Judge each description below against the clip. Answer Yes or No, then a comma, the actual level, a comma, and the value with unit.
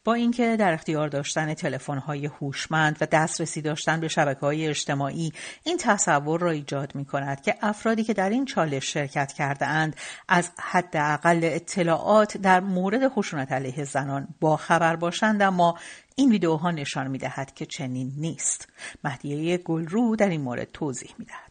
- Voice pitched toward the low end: No, medium, 160 Hz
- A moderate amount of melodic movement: Yes, average, 4.3 semitones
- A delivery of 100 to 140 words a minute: No, average, 150 wpm